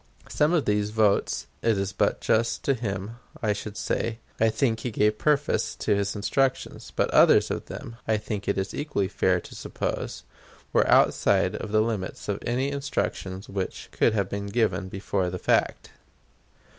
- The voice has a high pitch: No, low, 105 Hz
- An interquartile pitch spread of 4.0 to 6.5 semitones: No, average, 2.7 semitones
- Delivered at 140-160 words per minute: No, average, 175 wpm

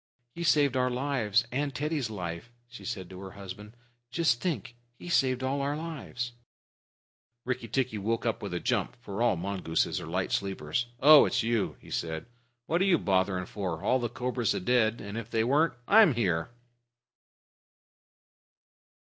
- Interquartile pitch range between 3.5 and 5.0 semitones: No, wide, 5.4 semitones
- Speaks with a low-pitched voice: Yes, low, 120 Hz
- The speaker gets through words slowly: No, average, 165 wpm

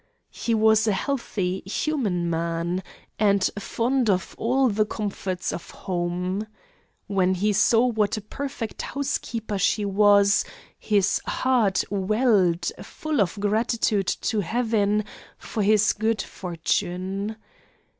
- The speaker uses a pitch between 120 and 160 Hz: No, high, 205 Hz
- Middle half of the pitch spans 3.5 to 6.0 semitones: No, average, 3.0 semitones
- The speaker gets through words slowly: Yes, slow, 115 wpm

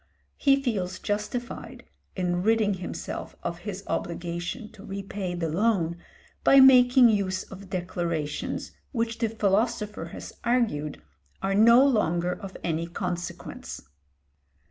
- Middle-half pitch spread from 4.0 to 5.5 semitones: Yes, average, 4.6 semitones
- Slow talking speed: Yes, slow, 120 wpm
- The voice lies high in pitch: Yes, high, 195 Hz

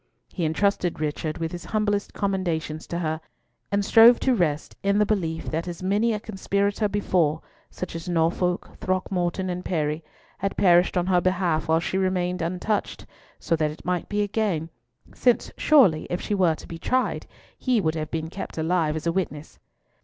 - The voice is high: No, medium, 180 Hz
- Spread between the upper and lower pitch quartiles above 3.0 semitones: Yes, average, 3.6 semitones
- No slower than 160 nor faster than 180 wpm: Yes, average, 170 wpm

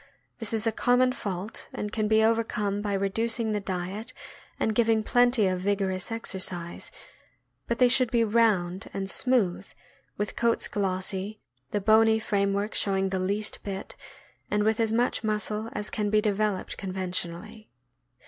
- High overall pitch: Yes, high, 210 Hz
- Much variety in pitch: No, narrow, 2.6 semitones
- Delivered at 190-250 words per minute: No, average, 160 wpm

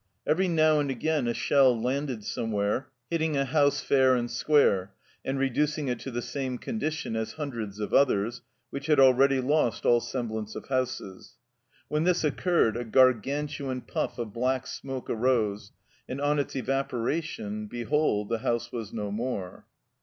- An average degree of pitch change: Yes, average, 3.9 semitones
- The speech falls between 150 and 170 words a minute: Yes, average, 165 wpm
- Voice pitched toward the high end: No, low, 130 Hz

